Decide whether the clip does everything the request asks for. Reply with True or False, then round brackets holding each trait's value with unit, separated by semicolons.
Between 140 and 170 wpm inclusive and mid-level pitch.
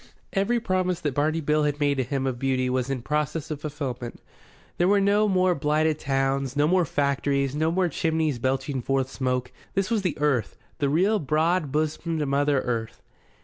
False (185 wpm; 150 Hz)